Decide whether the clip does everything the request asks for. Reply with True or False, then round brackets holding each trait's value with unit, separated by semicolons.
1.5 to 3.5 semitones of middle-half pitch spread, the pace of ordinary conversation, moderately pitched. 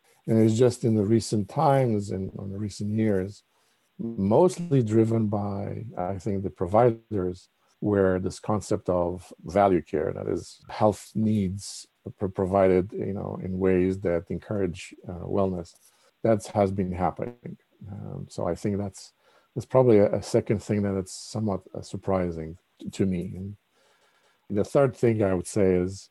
False (2.8 semitones; 155 wpm; 100 Hz)